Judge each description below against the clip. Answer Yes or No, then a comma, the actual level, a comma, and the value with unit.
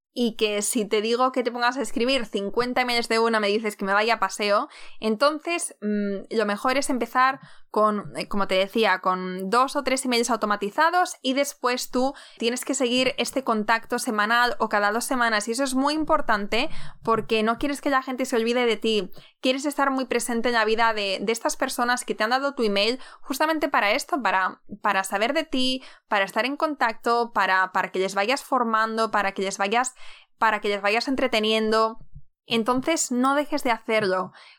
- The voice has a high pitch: Yes, high, 230 Hz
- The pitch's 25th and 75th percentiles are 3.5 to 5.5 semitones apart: Yes, average, 3.8 semitones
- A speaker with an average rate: No, fast, 200 wpm